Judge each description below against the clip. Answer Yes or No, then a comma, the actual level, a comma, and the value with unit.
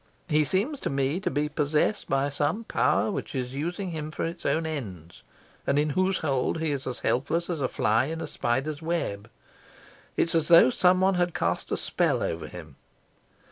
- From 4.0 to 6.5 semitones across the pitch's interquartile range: Yes, average, 4.3 semitones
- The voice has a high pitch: No, medium, 150 Hz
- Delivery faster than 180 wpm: Yes, average, 190 wpm